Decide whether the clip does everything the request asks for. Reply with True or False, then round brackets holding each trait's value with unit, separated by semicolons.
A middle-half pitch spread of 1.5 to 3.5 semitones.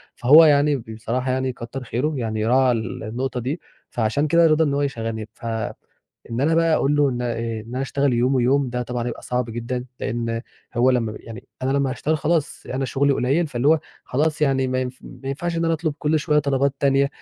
True (3.2 semitones)